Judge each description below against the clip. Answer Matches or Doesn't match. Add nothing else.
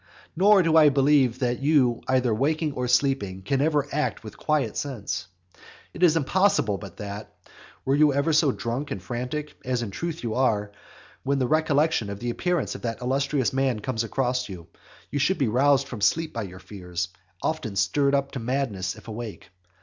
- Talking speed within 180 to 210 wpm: Matches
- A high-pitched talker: Doesn't match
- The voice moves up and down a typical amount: Matches